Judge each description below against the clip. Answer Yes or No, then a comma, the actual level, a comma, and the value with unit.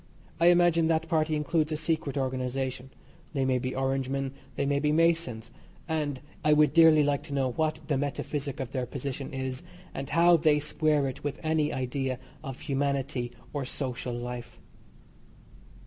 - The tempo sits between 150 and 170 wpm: No, average, 180 wpm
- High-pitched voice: No, medium, 140 Hz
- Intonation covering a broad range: No, average, 2.9 semitones